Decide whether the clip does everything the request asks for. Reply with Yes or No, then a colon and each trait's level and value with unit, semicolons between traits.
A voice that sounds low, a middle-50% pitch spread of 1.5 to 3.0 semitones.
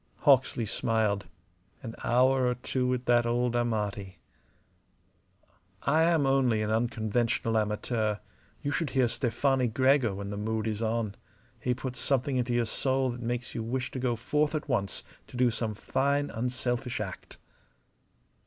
Yes: low, 120 Hz; average, 2.7 semitones